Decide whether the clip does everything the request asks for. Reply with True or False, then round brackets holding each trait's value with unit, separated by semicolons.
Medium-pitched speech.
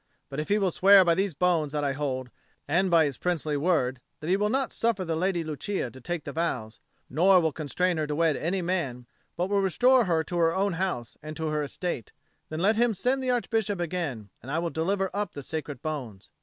True (170 Hz)